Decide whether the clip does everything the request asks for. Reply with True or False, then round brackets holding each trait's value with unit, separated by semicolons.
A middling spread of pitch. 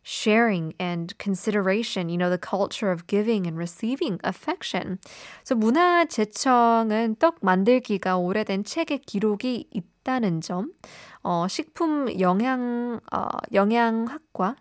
True (5.0 semitones)